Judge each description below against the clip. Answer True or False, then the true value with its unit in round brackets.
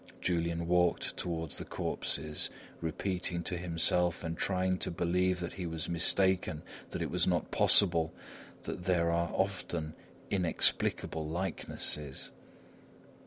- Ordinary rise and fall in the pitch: False (1.8 semitones)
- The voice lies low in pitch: True (85 Hz)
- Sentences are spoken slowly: True (120 wpm)